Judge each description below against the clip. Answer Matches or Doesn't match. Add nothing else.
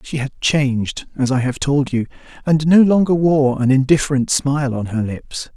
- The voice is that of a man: Matches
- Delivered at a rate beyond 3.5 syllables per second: Matches